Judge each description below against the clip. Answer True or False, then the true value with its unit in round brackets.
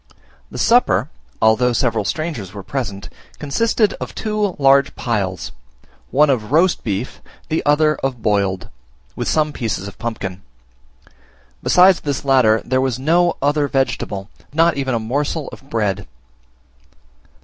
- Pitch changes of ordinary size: False (5.7 semitones)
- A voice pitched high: False (135 Hz)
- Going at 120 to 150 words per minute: True (140 wpm)